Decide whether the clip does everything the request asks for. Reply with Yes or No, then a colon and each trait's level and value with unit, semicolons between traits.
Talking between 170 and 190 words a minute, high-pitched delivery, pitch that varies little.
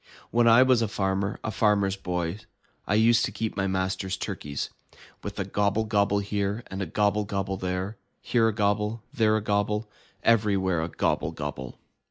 No: average, 175 wpm; low, 100 Hz; narrow, 2.2 semitones